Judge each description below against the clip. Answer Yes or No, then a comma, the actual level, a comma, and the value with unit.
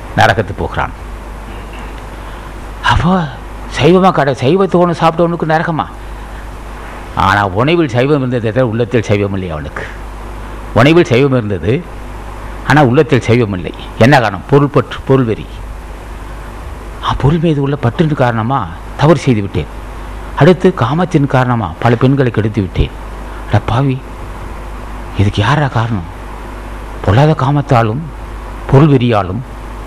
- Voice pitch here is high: No, low, 120 Hz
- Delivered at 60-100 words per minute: Yes, average, 95 wpm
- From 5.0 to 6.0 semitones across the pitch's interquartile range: Yes, wide, 5.4 semitones